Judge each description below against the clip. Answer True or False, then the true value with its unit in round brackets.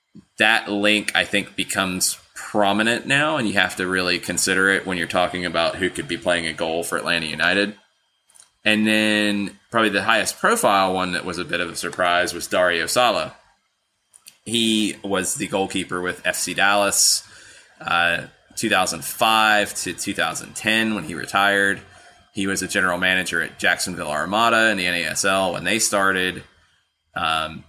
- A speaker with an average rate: True (160 wpm)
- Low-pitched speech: True (95 Hz)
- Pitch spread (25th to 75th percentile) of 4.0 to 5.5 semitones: False (2.7 semitones)